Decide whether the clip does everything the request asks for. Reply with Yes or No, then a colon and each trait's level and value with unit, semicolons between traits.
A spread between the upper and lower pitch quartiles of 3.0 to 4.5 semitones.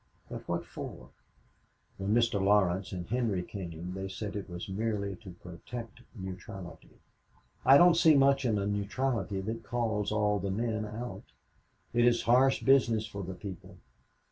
Yes: average, 3.6 semitones